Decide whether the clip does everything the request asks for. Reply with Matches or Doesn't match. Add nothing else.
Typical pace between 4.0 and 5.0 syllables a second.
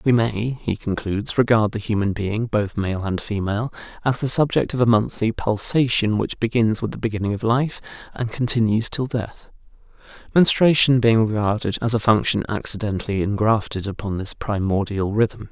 Doesn't match